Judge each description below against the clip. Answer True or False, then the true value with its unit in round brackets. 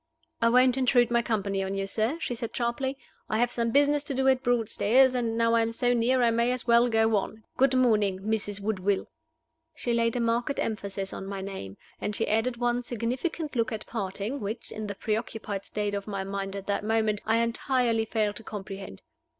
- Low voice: False (225 Hz)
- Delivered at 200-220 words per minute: True (205 wpm)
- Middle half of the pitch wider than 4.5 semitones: False (3.0 semitones)